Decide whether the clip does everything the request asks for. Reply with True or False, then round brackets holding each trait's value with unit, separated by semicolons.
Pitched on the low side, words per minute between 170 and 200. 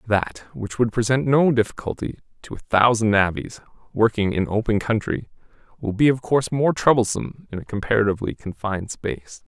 False (110 Hz; 155 wpm)